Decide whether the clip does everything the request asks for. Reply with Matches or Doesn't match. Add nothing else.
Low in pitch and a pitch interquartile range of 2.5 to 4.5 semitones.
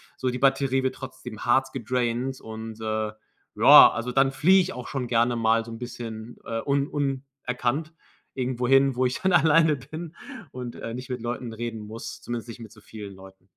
Matches